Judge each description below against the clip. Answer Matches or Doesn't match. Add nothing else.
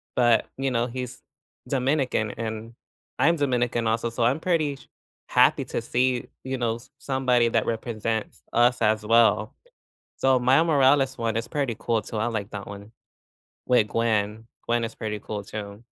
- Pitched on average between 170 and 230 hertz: Doesn't match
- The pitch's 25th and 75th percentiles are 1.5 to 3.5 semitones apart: Matches